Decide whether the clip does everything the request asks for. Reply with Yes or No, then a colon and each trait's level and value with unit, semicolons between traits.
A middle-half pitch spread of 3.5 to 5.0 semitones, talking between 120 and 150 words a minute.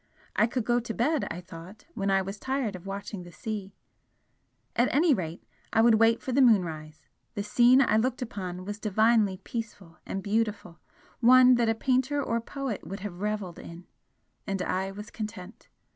No: average, 3.9 semitones; average, 180 wpm